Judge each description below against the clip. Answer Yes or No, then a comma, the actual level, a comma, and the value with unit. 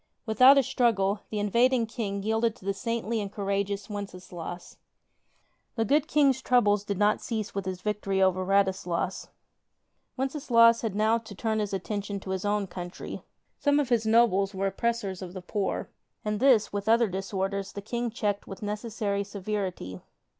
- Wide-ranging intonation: No, average, 2.9 semitones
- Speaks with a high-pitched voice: Yes, high, 205 Hz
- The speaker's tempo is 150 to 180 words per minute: Yes, average, 170 wpm